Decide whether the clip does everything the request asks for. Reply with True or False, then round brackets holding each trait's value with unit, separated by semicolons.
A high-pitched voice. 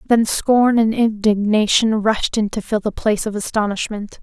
True (215 Hz)